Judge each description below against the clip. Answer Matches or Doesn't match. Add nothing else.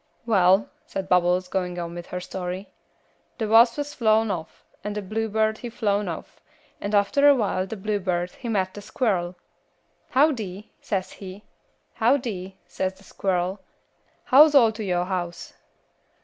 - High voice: Matches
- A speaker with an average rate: Matches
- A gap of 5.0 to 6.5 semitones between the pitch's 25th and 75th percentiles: Doesn't match